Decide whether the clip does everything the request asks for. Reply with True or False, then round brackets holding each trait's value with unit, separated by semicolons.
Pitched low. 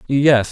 True (130 Hz)